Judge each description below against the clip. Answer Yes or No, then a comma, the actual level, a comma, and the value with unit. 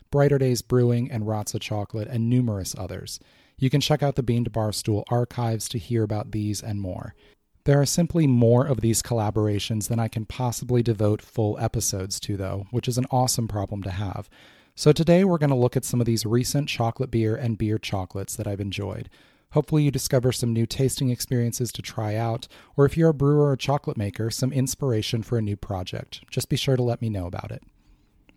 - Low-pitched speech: Yes, low, 115 Hz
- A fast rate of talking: Yes, fast, 210 wpm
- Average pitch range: Yes, average, 3.5 semitones